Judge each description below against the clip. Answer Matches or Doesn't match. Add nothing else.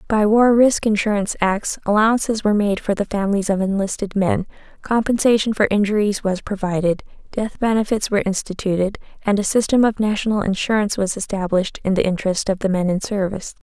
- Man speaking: Doesn't match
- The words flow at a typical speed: Matches